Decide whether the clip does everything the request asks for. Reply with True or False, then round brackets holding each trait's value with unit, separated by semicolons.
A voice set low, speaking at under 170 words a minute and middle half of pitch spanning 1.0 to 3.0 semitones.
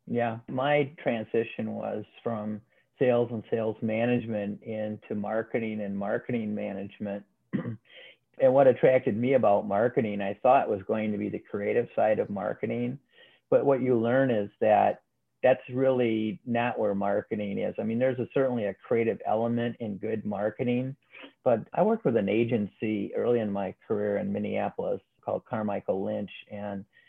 True (110 Hz; 155 wpm; 2.5 semitones)